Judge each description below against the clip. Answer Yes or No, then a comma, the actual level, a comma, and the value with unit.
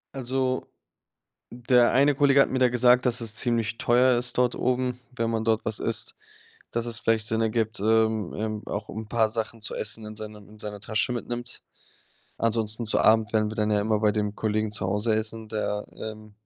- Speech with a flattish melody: Yes, narrow, 2.0 semitones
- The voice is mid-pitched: No, low, 110 Hz